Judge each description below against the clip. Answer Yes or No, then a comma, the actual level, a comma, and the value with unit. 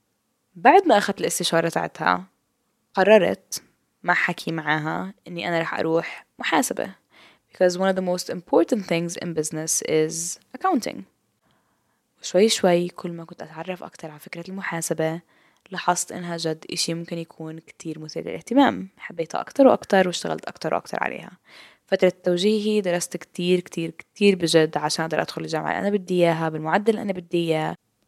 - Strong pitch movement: No, average, 2.8 semitones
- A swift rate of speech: Yes, fast, 150 wpm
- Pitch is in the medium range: Yes, medium, 175 Hz